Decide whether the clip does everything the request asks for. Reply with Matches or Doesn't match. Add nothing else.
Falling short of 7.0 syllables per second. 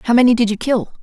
Doesn't match